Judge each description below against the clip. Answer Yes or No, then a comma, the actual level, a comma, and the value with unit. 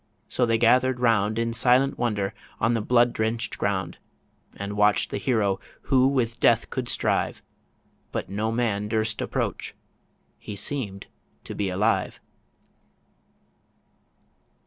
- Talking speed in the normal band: No, slow, 125 wpm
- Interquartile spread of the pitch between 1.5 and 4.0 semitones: Yes, average, 2.8 semitones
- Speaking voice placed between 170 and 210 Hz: No, low, 115 Hz